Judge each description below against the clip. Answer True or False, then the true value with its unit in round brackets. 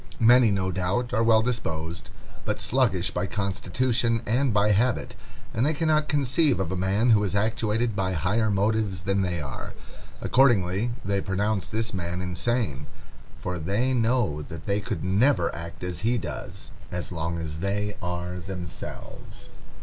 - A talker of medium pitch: False (100 Hz)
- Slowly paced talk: False (155 wpm)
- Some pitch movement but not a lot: True (4.4 semitones)